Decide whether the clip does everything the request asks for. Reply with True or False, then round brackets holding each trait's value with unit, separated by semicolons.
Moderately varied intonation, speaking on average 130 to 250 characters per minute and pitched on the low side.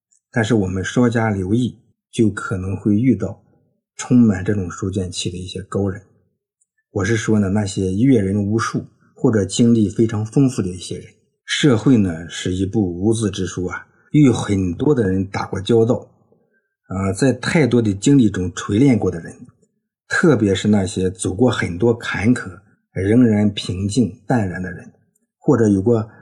True (4.0 semitones; 240 characters per minute; 110 Hz)